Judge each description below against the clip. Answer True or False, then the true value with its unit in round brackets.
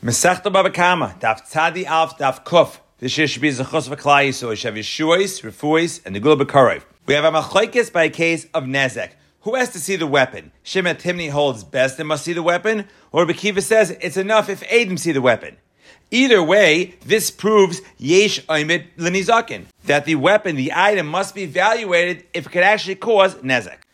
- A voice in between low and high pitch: True (170 Hz)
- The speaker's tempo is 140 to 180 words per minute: True (165 wpm)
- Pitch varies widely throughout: False (4.7 semitones)